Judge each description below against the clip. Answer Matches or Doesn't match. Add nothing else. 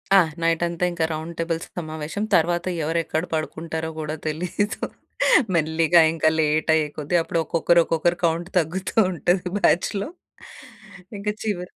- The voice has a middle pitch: Matches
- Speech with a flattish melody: Matches